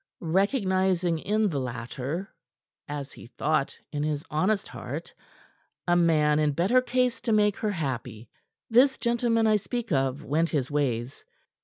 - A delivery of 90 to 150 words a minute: Yes, average, 145 wpm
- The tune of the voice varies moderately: No, wide, 7.0 semitones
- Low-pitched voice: No, medium, 170 Hz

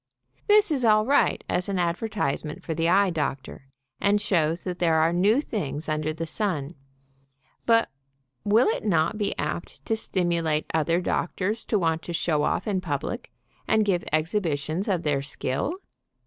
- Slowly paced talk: No, average, 165 wpm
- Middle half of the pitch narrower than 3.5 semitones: No, average, 4.9 semitones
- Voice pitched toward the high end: No, medium, 175 Hz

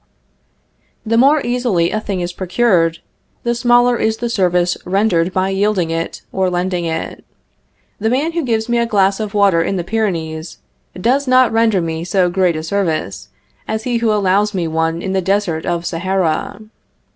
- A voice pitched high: Yes, high, 195 Hz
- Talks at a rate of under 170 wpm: No, average, 175 wpm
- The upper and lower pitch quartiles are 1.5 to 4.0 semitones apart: No, average, 4.4 semitones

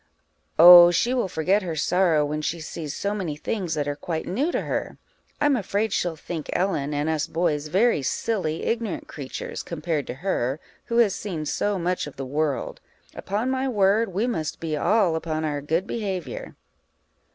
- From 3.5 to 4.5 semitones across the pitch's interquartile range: No, average, 4.9 semitones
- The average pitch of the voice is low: No, medium, 175 Hz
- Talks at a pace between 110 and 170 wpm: No, average, 185 wpm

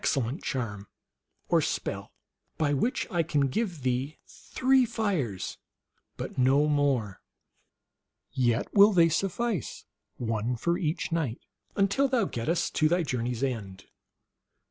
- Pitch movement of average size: No, wide, 6.8 semitones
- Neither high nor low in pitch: Yes, medium, 145 Hz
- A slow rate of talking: Yes, slow, 125 wpm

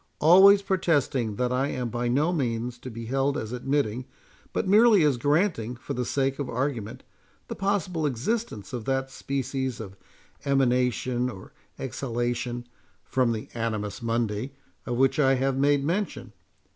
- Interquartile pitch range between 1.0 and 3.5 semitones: Yes, average, 3.2 semitones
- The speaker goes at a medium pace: Yes, average, 150 wpm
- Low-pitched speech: Yes, low, 130 Hz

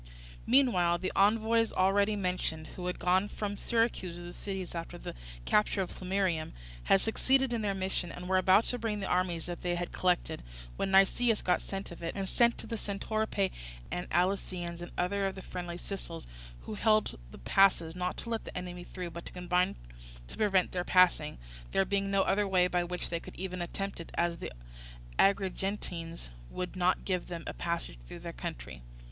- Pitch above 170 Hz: Yes, medium, 185 Hz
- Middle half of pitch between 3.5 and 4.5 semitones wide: No, narrow, 2.4 semitones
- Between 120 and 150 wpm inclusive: No, average, 195 wpm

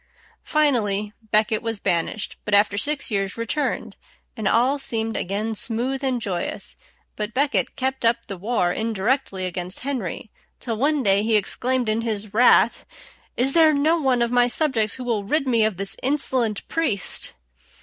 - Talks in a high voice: Yes, high, 230 Hz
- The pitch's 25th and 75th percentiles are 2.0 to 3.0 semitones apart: No, average, 4.2 semitones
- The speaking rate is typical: Yes, average, 165 wpm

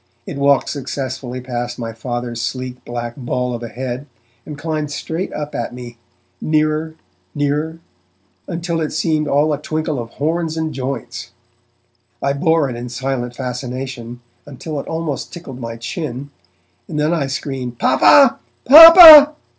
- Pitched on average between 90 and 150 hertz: Yes, medium, 140 Hz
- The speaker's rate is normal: Yes, average, 145 wpm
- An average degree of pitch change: Yes, average, 4.1 semitones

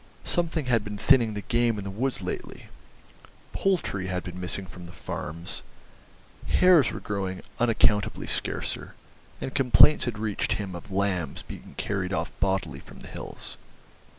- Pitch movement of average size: Yes, average, 4.6 semitones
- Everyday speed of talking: Yes, average, 150 wpm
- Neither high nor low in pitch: No, low, 100 Hz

